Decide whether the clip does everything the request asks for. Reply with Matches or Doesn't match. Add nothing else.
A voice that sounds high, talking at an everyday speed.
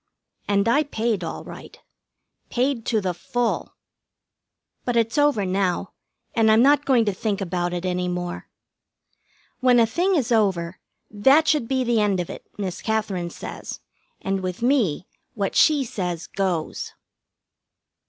Matches